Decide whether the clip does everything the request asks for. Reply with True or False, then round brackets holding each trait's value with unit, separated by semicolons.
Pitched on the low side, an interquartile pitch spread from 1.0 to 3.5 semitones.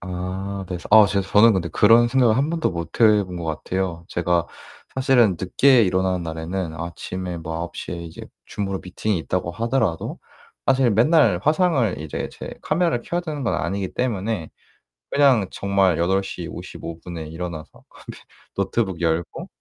False (95 Hz; 5.1 semitones)